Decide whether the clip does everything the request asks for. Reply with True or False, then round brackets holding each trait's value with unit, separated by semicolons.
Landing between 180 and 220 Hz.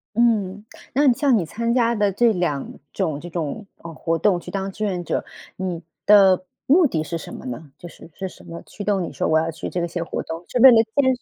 True (190 Hz)